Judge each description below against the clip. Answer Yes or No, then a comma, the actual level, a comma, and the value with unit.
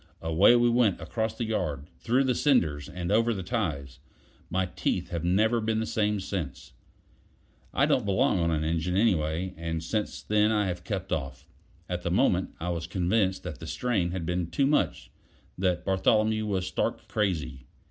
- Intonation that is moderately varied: Yes, average, 4.7 semitones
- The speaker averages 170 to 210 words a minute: Yes, average, 180 wpm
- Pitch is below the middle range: Yes, very low, 95 Hz